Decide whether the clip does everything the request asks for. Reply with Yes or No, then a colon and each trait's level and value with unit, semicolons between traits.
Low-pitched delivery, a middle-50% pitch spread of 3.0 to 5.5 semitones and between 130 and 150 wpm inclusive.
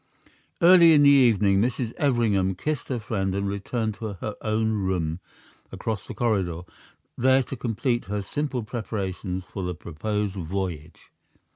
Yes: low, 105 Hz; average, 4.2 semitones; average, 145 wpm